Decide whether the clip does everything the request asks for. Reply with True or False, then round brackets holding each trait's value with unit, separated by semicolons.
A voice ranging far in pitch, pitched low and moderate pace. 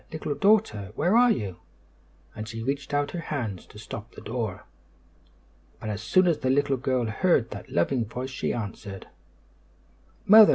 True (5.7 semitones; 125 Hz; 165 wpm)